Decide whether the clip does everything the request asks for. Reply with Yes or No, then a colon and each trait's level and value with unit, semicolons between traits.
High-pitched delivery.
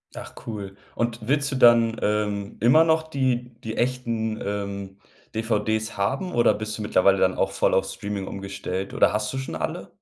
No: low, 110 Hz